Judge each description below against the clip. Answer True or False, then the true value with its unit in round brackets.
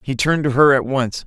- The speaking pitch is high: False (135 Hz)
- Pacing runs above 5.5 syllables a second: True (6.0 syllables/s)